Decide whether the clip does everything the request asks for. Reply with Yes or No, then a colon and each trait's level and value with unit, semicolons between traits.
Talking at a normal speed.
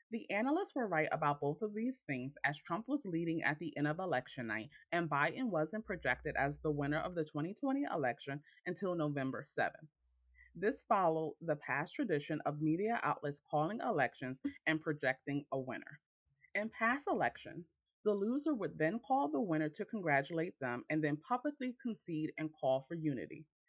Yes: average, 170 wpm